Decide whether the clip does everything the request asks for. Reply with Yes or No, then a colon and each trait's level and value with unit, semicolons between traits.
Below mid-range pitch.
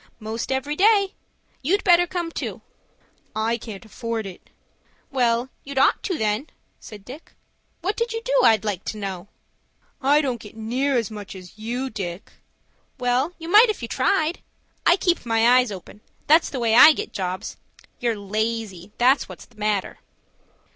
No: high, 240 Hz